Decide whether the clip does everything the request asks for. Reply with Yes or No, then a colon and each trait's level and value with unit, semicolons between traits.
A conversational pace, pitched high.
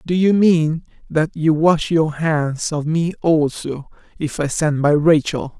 No: average, 170 wpm; medium, 155 Hz